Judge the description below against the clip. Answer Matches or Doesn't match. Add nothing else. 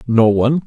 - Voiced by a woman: Doesn't match